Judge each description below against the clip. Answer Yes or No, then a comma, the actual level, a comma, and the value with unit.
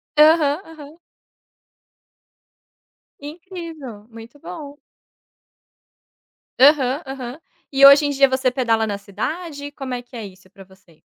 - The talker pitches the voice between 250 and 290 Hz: Yes, very high, 275 Hz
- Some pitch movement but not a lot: Yes, average, 4.8 semitones